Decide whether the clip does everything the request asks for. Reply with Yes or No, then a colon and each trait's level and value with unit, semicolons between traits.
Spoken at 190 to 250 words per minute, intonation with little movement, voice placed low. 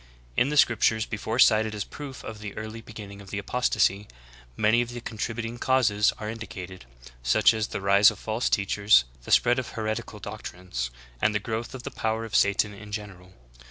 Yes: average, 195 wpm; narrow, 2.2 semitones; low, 110 Hz